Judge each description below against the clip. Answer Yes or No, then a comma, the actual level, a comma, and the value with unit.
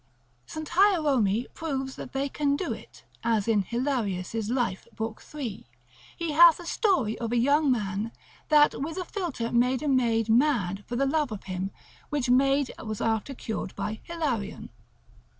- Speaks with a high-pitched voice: Yes, very high, 255 Hz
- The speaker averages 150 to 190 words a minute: Yes, average, 170 wpm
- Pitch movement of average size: Yes, average, 5.0 semitones